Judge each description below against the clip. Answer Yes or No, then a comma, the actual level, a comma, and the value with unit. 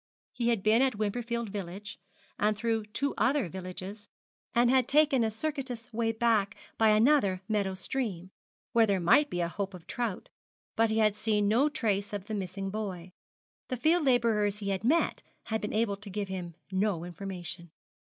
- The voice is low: No, high, 210 Hz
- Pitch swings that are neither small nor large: Yes, average, 3.3 semitones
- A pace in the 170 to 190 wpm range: Yes, average, 180 wpm